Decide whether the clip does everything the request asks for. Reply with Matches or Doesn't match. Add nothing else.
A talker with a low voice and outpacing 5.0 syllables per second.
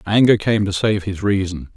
Doesn't match